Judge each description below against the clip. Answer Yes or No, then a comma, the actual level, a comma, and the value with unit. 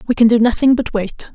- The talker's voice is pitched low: No, high, 230 Hz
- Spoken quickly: Yes, fast, 265 wpm